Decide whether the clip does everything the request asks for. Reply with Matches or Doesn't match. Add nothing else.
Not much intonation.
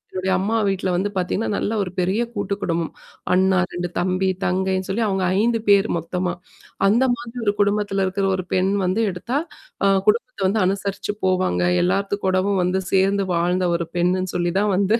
Matches